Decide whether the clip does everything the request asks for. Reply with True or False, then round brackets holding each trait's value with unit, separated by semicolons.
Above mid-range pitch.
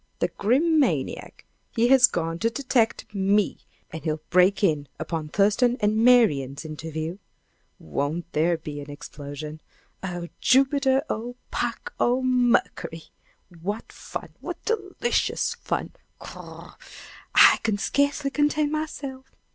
True (205 Hz)